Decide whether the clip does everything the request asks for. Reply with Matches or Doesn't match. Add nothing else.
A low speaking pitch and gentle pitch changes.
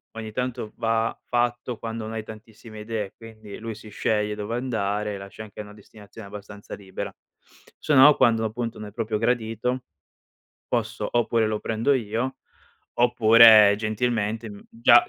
Matches